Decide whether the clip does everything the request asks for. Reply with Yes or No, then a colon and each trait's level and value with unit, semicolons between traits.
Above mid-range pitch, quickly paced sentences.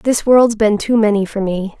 Yes: high, 215 Hz; fast, 235 wpm